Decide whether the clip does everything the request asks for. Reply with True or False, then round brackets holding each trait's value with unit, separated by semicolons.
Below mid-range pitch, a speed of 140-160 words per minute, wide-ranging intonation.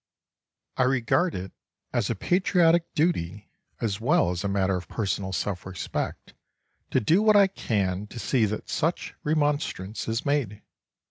True (115 Hz; 150 wpm; 8.4 semitones)